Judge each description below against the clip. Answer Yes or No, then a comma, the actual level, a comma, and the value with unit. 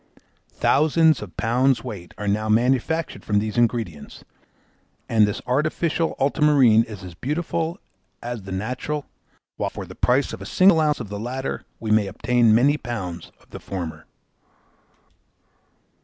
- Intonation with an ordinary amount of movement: No, wide, 5.8 semitones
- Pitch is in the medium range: No, low, 120 Hz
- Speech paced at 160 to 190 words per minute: No, average, 145 wpm